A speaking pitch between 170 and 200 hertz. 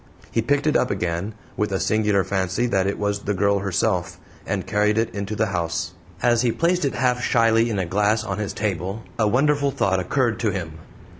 No: low, 105 Hz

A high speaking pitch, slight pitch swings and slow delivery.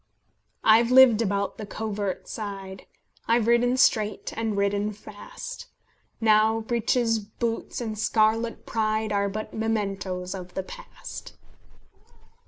Yes: high, 215 Hz; narrow, 2.1 semitones; slow, 115 wpm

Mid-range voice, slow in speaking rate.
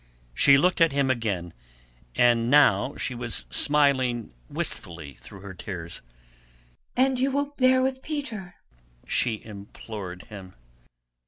No: low, 120 Hz; slow, 120 wpm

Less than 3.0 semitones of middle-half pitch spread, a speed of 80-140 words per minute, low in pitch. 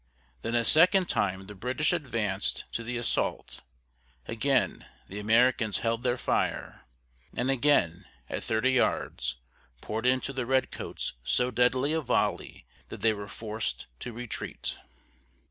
No: average, 3.4 semitones; slow, 135 wpm; low, 120 Hz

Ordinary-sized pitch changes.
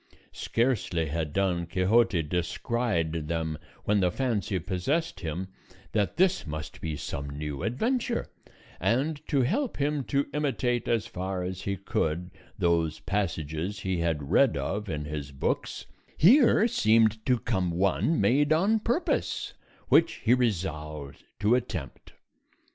No: wide, 7.3 semitones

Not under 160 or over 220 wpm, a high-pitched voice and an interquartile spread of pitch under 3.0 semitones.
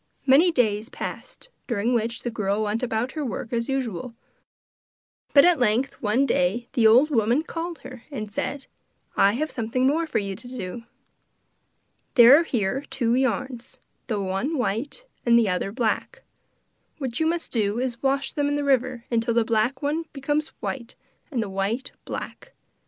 No: average, 170 wpm; high, 245 Hz; average, 3.9 semitones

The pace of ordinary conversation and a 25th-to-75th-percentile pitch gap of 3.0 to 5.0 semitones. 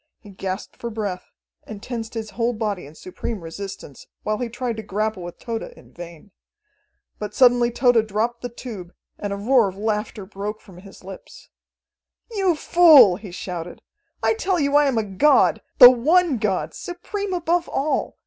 Yes: average, 175 wpm; average, 4.4 semitones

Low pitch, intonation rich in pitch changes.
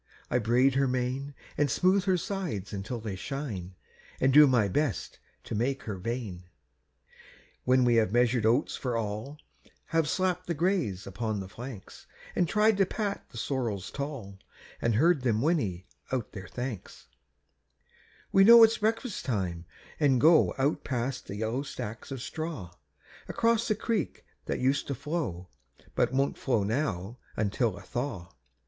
Yes: low, 125 Hz; wide, 6.1 semitones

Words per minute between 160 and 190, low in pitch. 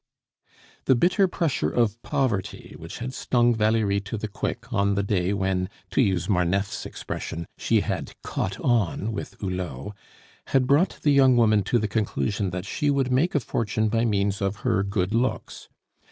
Yes: average, 170 wpm; low, 105 Hz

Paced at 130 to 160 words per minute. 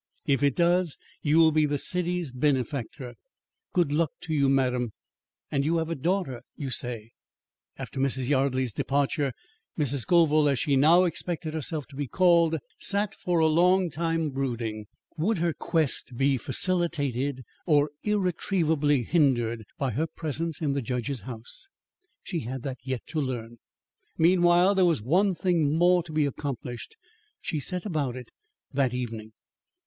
Yes: average, 155 wpm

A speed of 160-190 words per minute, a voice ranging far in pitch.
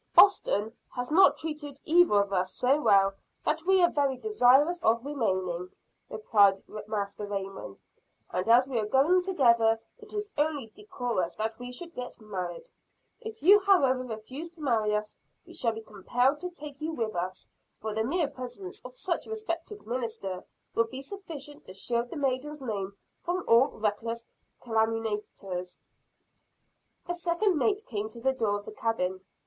Yes: average, 165 wpm; wide, 6.5 semitones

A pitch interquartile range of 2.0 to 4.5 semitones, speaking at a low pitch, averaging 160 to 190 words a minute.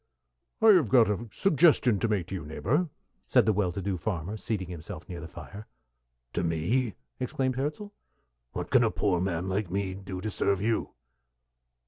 No: average, 5.1 semitones; low, 100 Hz; average, 180 wpm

